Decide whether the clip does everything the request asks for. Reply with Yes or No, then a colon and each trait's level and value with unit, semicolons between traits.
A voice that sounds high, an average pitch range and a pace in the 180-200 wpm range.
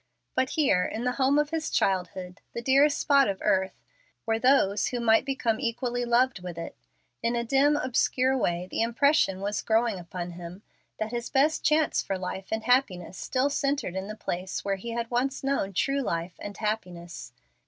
No: high, 230 Hz; wide, 5.9 semitones; average, 185 wpm